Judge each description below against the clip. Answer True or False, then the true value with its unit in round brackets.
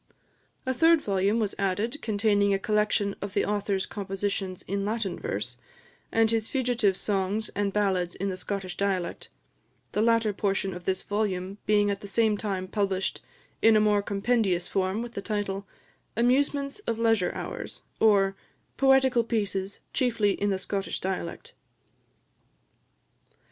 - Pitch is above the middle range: True (205 Hz)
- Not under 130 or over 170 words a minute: True (145 wpm)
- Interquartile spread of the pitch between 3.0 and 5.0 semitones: False (2.5 semitones)